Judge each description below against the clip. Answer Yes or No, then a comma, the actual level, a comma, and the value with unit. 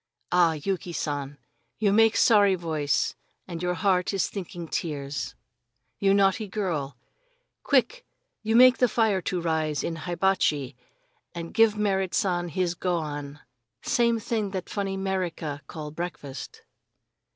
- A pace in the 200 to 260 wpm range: No, average, 140 wpm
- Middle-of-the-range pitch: Yes, medium, 180 Hz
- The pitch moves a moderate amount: Yes, average, 4.3 semitones